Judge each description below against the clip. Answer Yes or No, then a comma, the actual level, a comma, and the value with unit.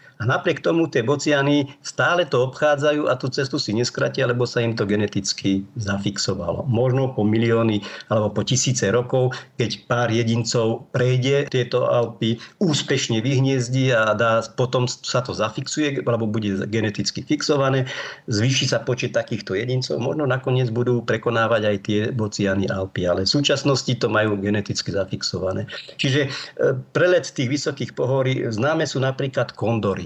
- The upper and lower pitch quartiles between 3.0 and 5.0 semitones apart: Yes, average, 3.8 semitones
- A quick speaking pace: No, average, 145 wpm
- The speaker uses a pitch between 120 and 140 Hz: Yes, low, 125 Hz